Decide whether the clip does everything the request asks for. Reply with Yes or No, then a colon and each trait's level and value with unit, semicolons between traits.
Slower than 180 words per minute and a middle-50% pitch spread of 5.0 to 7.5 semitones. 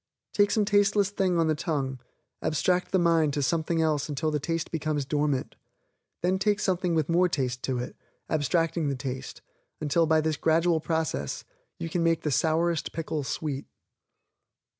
No: average, 165 wpm; average, 2.7 semitones